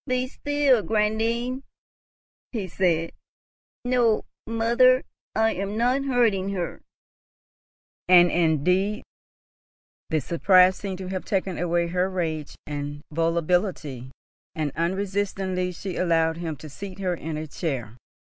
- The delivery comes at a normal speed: No, slow, 120 wpm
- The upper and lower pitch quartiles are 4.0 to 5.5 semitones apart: Yes, average, 4.6 semitones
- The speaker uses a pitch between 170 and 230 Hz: Yes, medium, 185 Hz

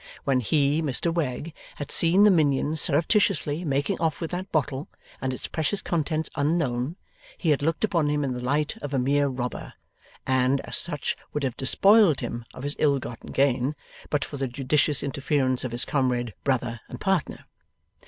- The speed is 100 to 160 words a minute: No, average, 180 wpm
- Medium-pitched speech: Yes, medium, 145 Hz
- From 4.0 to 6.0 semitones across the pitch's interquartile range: No, average, 3.4 semitones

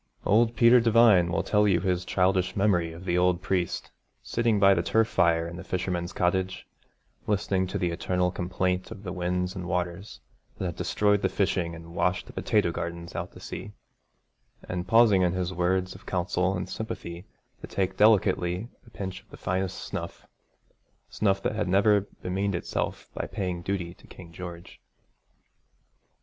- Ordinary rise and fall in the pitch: No, narrow, 2.2 semitones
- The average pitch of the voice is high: No, very low, 95 Hz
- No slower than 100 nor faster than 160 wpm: No, average, 170 wpm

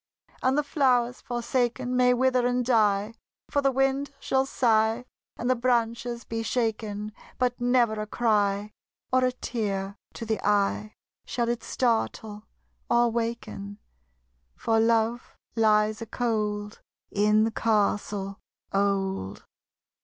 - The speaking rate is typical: No, slow, 125 wpm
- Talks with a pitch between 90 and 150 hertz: No, high, 230 Hz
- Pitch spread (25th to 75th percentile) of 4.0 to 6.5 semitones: No, average, 2.7 semitones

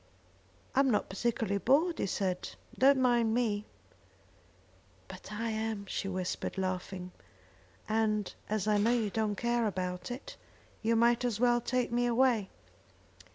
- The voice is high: Yes, high, 220 Hz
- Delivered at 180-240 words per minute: No, average, 140 wpm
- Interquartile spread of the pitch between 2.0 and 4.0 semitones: Yes, average, 3.1 semitones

